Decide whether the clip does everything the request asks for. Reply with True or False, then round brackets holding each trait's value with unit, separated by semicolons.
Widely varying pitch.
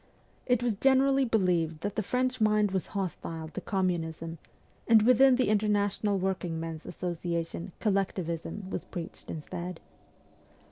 False (4.2 semitones)